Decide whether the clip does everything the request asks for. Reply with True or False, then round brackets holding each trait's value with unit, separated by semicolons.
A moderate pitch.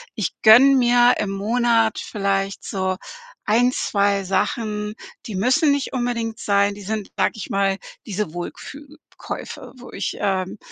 False (215 Hz)